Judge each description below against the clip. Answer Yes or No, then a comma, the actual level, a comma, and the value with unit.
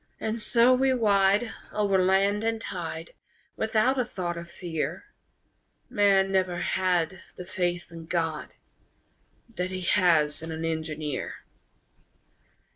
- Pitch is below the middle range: No, medium, 185 Hz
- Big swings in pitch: No, average, 3.7 semitones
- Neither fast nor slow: No, slow, 120 wpm